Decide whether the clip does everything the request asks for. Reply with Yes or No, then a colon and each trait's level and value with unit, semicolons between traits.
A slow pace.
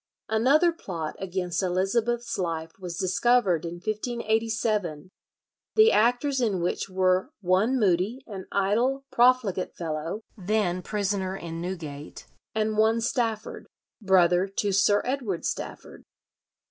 Yes: slow, 115 wpm